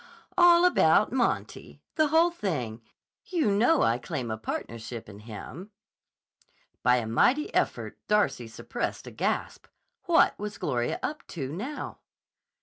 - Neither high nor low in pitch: Yes, medium, 170 Hz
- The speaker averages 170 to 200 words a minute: No, slow, 135 wpm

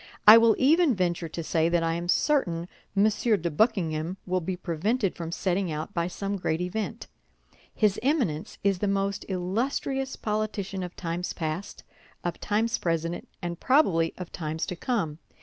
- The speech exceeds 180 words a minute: No, average, 165 wpm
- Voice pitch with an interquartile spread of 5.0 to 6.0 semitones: No, average, 4.3 semitones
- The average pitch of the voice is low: No, medium, 185 Hz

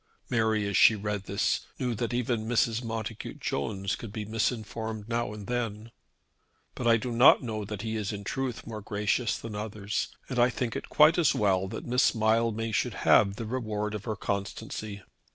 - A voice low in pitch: Yes, low, 110 Hz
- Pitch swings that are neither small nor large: No, narrow, 2.1 semitones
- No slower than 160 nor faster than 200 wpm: Yes, average, 190 wpm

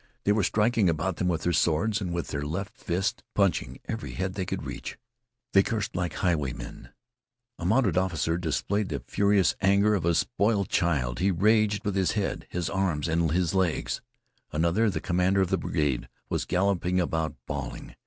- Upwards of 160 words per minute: Yes, average, 180 wpm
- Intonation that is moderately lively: Yes, average, 3.3 semitones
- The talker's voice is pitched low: Yes, very low, 90 Hz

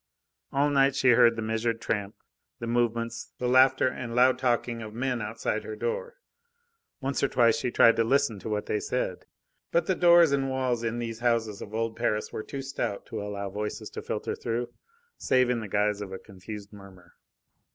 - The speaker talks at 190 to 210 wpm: Yes, average, 195 wpm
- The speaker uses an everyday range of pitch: Yes, average, 3.4 semitones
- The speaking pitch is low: Yes, low, 115 Hz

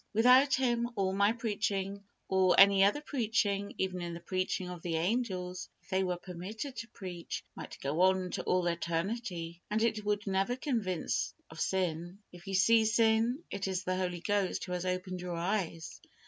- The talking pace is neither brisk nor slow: Yes, average, 175 wpm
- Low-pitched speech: No, high, 190 Hz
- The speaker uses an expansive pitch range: No, average, 3.4 semitones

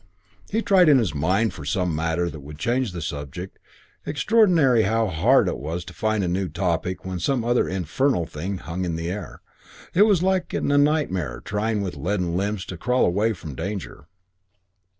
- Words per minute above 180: Yes, average, 190 wpm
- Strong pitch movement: Yes, wide, 6.3 semitones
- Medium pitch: No, very low, 95 Hz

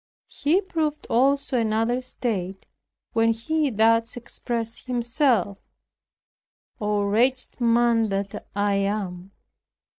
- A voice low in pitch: No, high, 230 Hz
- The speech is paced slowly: Yes, slow, 95 wpm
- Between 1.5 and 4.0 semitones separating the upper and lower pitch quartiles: Yes, average, 3.6 semitones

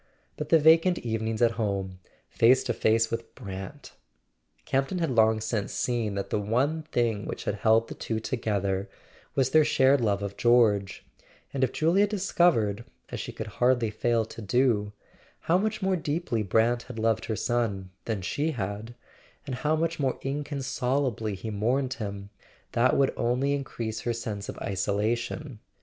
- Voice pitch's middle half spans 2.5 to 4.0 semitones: No, average, 4.4 semitones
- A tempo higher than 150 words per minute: Yes, average, 165 wpm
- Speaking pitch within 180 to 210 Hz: No, low, 115 Hz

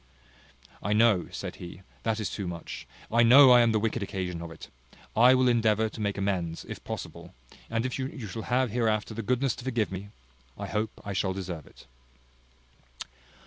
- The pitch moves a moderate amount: Yes, average, 3.5 semitones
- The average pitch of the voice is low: Yes, low, 110 Hz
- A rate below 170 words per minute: No, average, 185 wpm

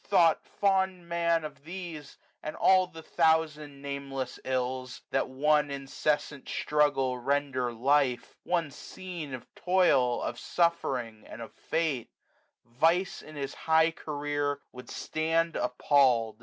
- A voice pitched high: No, medium, 145 Hz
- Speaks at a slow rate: Yes, slow, 130 wpm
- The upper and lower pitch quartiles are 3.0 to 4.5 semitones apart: Yes, average, 4.0 semitones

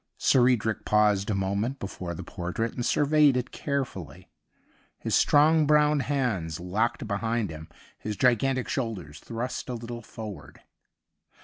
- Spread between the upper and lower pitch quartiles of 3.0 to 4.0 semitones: No, average, 5.0 semitones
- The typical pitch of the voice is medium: No, low, 115 Hz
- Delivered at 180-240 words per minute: No, slow, 135 wpm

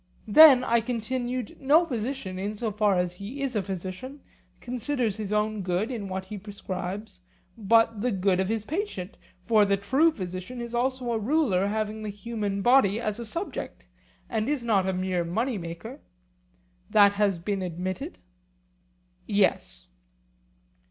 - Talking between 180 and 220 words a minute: No, average, 155 wpm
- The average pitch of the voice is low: No, high, 215 Hz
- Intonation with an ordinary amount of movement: Yes, average, 4.2 semitones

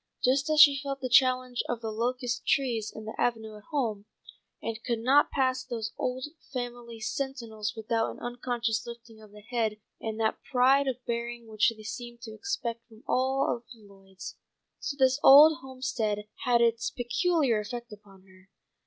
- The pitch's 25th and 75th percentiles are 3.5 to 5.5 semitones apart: No, average, 2.8 semitones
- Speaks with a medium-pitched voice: No, high, 240 Hz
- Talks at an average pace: Yes, average, 170 wpm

